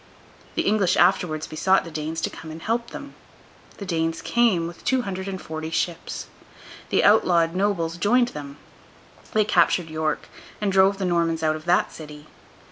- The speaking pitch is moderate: Yes, medium, 175 Hz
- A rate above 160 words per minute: Yes, average, 170 wpm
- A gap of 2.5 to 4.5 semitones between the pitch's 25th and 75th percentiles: Yes, average, 3.7 semitones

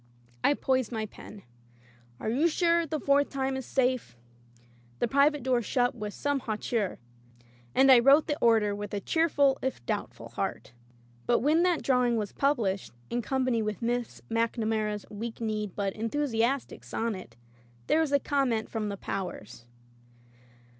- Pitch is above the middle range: Yes, high, 240 Hz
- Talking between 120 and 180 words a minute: Yes, average, 155 wpm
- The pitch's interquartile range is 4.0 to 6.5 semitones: Yes, average, 4.4 semitones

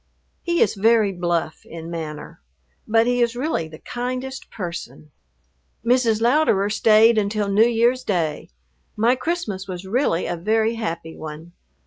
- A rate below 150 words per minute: Yes, average, 140 wpm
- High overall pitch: Yes, high, 215 Hz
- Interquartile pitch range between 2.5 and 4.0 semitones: No, wide, 5.6 semitones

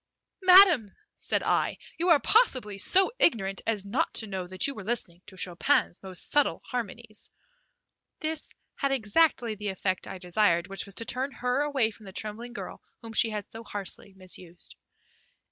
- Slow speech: No, average, 170 wpm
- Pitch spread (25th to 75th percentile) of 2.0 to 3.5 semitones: No, wide, 5.6 semitones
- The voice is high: Yes, high, 215 Hz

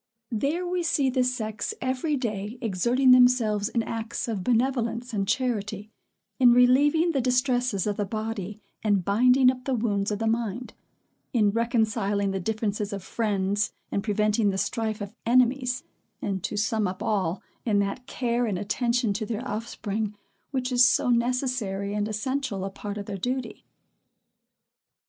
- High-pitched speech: Yes, high, 225 Hz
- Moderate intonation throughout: Yes, average, 3.5 semitones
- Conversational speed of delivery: Yes, average, 160 wpm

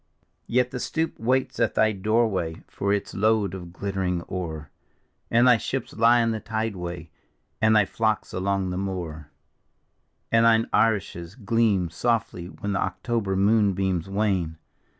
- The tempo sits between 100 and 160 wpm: Yes, average, 150 wpm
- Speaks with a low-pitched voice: Yes, low, 100 Hz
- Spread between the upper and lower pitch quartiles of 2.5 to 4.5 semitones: Yes, average, 3.8 semitones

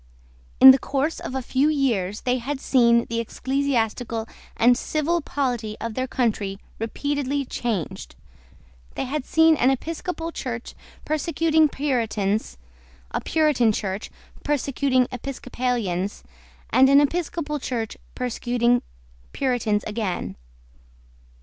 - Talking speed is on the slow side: Yes, slow, 110 wpm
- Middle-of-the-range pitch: No, very high, 255 Hz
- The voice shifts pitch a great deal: No, average, 3.9 semitones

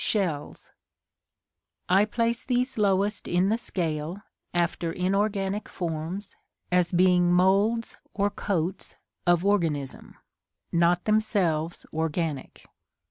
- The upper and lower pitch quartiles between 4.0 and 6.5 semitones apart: No, average, 3.4 semitones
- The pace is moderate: No, slow, 95 wpm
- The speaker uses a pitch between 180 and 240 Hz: Yes, medium, 185 Hz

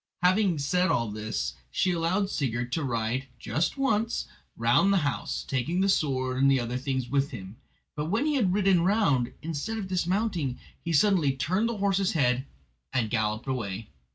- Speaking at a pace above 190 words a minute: No, average, 170 wpm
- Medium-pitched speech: Yes, medium, 145 Hz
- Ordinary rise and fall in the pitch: No, wide, 7.4 semitones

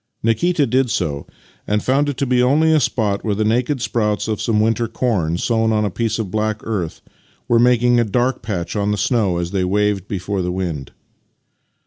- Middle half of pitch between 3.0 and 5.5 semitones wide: Yes, average, 3.6 semitones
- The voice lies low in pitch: Yes, low, 110 Hz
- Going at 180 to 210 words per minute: Yes, average, 200 wpm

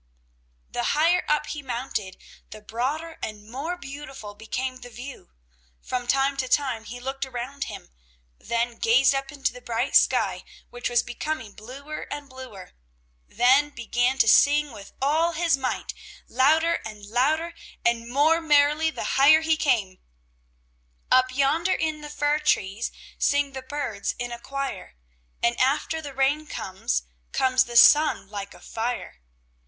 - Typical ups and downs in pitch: Yes, average, 3.8 semitones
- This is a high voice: Yes, very high, 265 Hz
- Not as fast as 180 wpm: Yes, average, 150 wpm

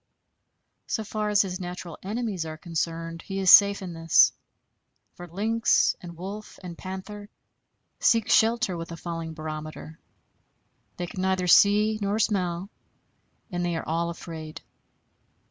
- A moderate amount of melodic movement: Yes, average, 3.5 semitones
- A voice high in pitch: No, medium, 180 Hz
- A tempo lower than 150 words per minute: Yes, average, 140 wpm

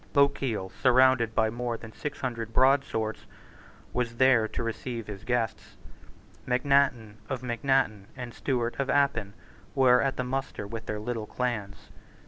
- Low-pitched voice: Yes, low, 120 Hz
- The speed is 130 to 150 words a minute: Yes, average, 140 wpm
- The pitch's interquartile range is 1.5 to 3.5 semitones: Yes, average, 2.8 semitones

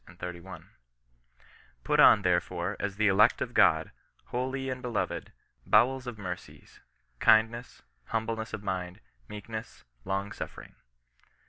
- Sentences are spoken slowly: Yes, slow, 120 wpm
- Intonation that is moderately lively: Yes, average, 3.8 semitones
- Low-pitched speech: Yes, low, 105 Hz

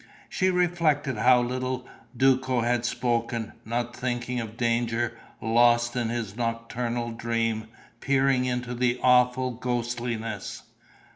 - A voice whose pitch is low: Yes, low, 120 Hz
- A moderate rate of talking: No, slow, 115 wpm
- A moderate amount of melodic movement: No, narrow, 1.4 semitones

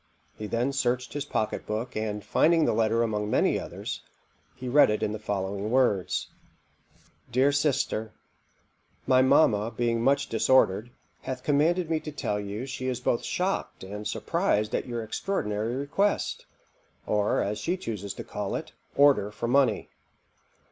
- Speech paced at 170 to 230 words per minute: No, average, 155 wpm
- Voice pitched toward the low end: Yes, low, 115 Hz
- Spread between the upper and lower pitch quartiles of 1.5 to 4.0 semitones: No, average, 4.7 semitones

